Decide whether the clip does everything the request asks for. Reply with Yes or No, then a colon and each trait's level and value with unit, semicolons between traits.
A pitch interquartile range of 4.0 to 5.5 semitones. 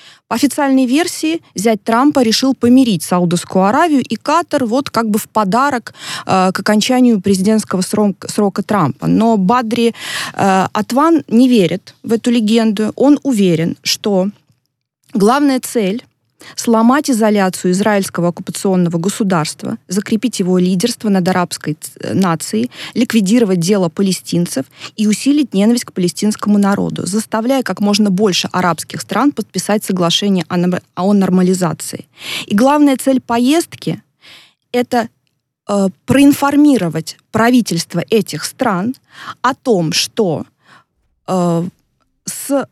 Yes: average, 4.8 semitones